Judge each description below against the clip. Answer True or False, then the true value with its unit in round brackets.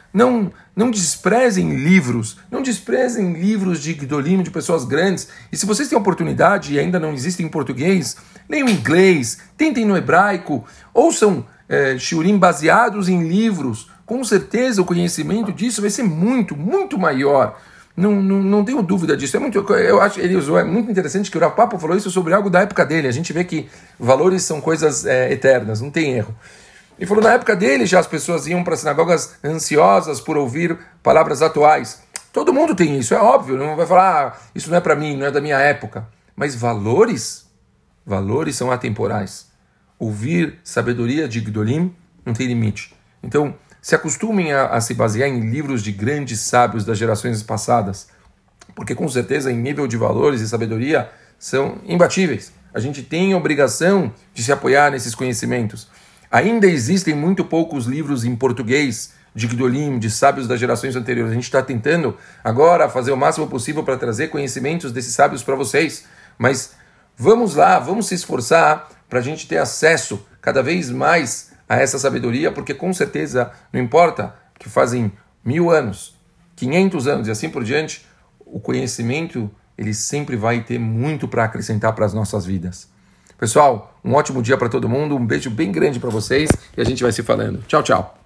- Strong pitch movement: True (6.9 semitones)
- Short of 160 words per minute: False (180 wpm)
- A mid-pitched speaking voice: True (150 Hz)